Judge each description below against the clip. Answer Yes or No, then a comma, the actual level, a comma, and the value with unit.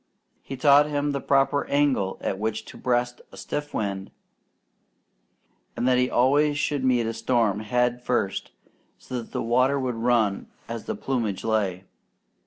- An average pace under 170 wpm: Yes, average, 160 wpm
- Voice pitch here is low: Yes, low, 125 Hz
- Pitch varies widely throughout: No, average, 3.5 semitones